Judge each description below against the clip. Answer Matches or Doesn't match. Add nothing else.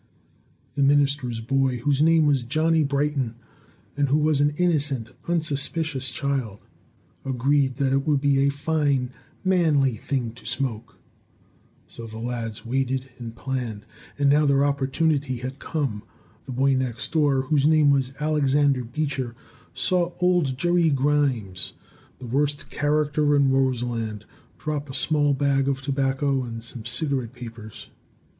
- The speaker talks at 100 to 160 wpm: Matches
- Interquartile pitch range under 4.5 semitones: Matches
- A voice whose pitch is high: Doesn't match